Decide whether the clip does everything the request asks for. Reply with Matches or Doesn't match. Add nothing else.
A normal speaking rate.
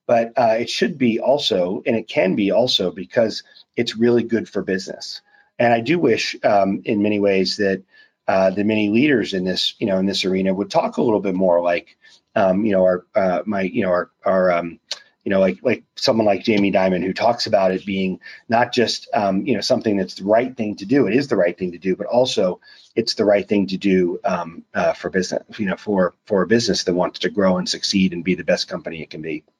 Doesn't match